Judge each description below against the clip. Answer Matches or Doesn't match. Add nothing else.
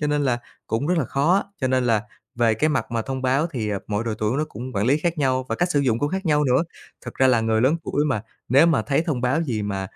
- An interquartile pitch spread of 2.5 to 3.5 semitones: Doesn't match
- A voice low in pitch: Matches